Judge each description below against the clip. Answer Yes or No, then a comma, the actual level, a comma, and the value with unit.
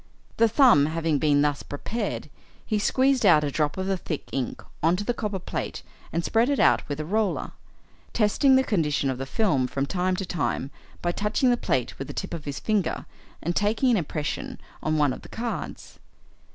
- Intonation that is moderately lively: No, wide, 6.8 semitones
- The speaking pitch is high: No, medium, 175 Hz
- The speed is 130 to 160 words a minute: No, fast, 205 wpm